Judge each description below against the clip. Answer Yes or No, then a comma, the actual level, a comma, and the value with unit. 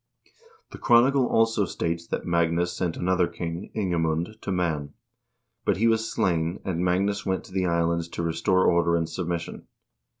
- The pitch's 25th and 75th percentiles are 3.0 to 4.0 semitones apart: No, narrow, 2.4 semitones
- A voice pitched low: Yes, very low, 90 Hz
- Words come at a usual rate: Yes, average, 160 wpm